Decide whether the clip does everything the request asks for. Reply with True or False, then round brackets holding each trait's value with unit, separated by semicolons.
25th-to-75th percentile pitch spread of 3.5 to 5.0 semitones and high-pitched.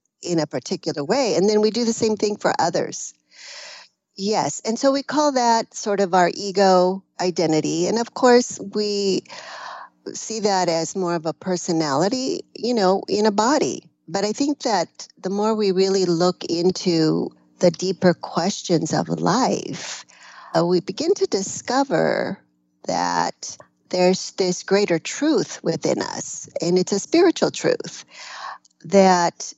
True (4.3 semitones; 195 Hz)